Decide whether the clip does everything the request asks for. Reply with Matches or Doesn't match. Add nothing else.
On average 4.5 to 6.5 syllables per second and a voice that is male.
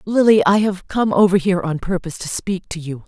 Doesn't match